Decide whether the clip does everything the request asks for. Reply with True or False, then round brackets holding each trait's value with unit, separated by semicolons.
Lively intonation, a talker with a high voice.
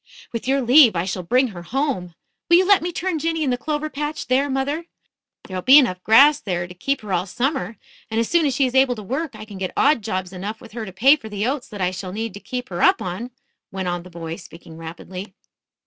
True (6.9 semitones; 225 Hz)